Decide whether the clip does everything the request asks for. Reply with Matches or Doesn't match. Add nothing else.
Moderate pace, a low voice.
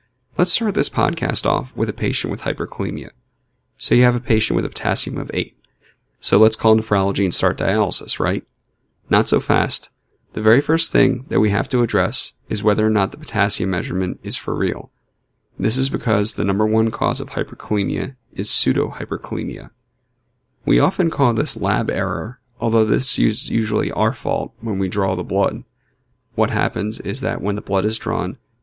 Matches